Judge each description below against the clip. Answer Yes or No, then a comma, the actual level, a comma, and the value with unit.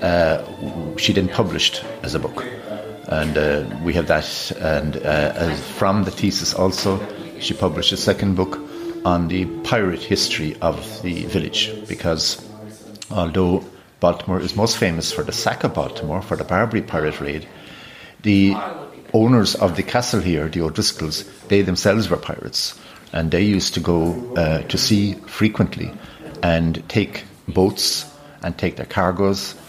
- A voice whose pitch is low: Yes, very low, 95 Hz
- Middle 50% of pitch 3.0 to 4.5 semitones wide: Yes, average, 3.9 semitones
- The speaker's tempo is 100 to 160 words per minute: Yes, average, 150 wpm